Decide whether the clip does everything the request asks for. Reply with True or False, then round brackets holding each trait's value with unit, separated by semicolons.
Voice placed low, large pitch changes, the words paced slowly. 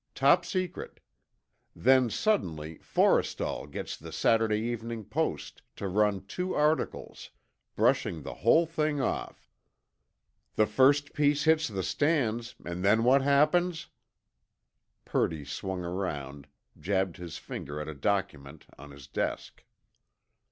True (110 Hz; 8.9 semitones; 115 wpm)